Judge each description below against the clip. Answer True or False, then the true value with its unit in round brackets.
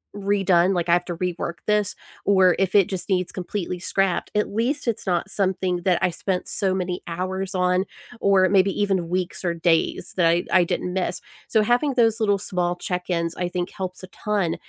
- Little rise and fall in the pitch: True (2.0 semitones)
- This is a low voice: False (185 Hz)